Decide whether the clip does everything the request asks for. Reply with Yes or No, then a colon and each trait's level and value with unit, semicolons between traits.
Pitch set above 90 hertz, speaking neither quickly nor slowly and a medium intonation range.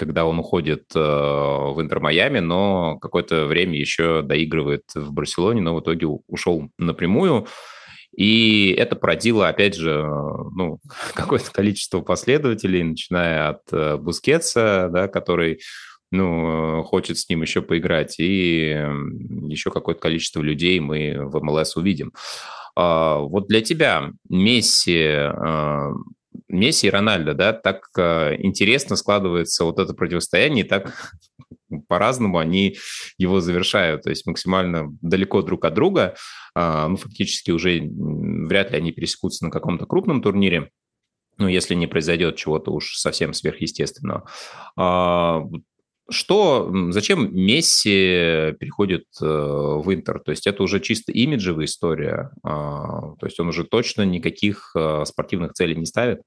No: very low, 85 Hz; average, 125 wpm; average, 3.7 semitones